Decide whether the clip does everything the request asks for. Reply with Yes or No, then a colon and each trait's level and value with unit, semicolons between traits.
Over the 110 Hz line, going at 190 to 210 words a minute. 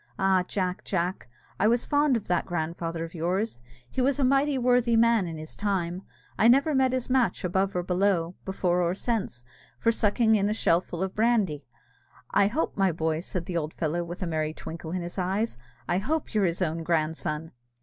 Yes: medium, 185 Hz; average, 200 wpm